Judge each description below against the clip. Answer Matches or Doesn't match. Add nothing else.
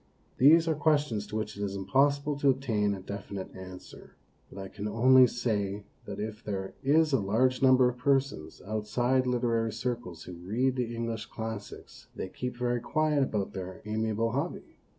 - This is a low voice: Matches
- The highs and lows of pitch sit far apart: Doesn't match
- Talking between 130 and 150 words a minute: Doesn't match